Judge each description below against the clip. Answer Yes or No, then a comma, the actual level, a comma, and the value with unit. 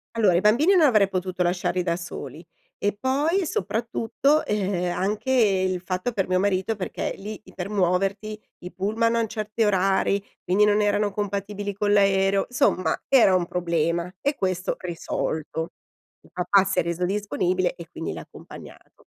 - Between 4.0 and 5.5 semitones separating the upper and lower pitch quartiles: No, average, 2.7 semitones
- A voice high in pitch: Yes, high, 195 Hz